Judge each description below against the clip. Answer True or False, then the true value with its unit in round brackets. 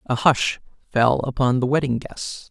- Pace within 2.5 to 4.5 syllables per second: True (4.3 syllables/s)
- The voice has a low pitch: True (125 Hz)